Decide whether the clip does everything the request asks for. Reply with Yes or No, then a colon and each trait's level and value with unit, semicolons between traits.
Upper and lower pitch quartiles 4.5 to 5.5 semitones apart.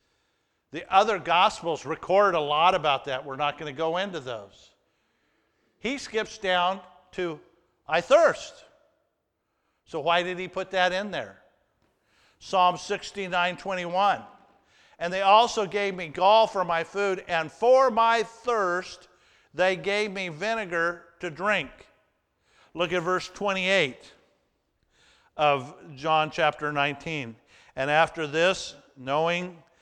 No: average, 3.3 semitones